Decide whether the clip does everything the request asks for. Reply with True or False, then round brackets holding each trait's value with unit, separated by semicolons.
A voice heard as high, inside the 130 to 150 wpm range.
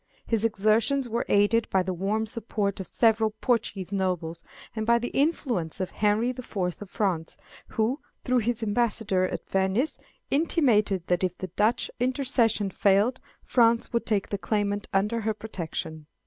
False (215 Hz; 160 wpm)